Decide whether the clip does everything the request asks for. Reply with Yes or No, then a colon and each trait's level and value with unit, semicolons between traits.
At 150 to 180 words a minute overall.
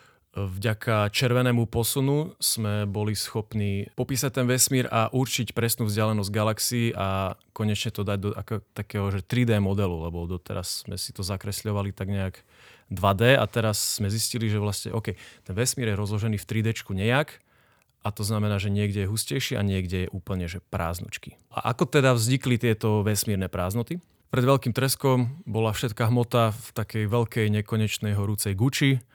Yes: average, 160 wpm